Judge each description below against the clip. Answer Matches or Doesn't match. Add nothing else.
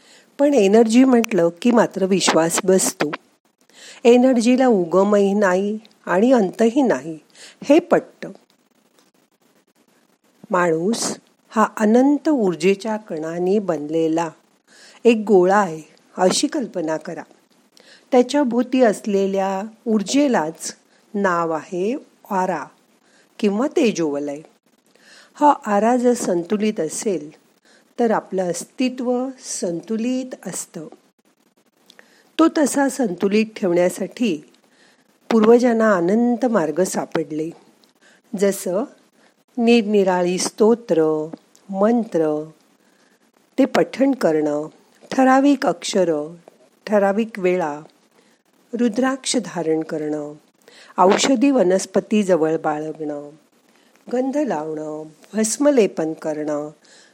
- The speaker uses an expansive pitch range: Matches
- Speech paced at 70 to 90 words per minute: Matches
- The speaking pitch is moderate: Doesn't match